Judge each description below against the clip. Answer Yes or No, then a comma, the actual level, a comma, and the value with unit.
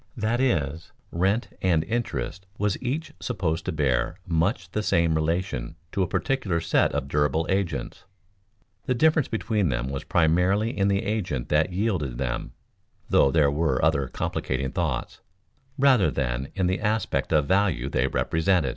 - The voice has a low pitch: Yes, very low, 85 Hz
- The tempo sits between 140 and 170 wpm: Yes, average, 155 wpm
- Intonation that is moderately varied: No, wide, 6.1 semitones